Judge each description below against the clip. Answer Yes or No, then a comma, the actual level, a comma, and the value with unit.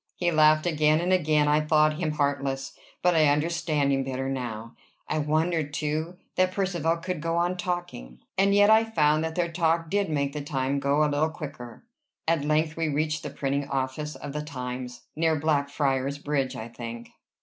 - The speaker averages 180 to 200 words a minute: Yes, average, 185 wpm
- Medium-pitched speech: Yes, medium, 150 Hz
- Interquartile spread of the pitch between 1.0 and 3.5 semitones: Yes, average, 2.9 semitones